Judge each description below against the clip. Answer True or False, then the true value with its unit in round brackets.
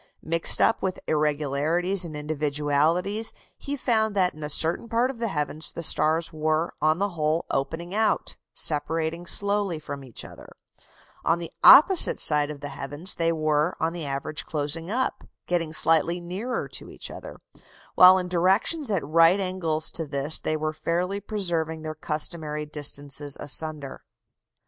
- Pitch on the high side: False (160 Hz)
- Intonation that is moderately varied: True (3.3 semitones)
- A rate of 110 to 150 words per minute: False (160 wpm)